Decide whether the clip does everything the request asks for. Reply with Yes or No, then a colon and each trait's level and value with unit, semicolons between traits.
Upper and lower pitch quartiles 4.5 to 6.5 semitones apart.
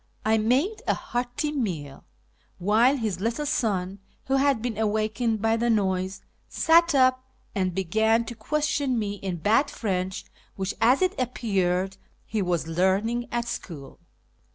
Yes: average, 4.8 semitones